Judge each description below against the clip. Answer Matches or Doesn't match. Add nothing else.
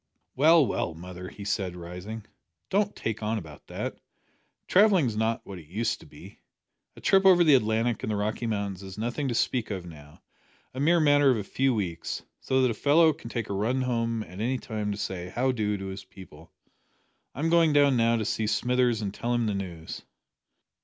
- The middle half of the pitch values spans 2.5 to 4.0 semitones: Doesn't match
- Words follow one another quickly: Matches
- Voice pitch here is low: Matches